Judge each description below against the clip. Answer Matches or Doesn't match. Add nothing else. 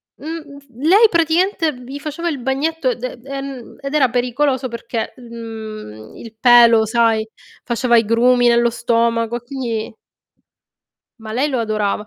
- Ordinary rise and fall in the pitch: Matches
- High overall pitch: Matches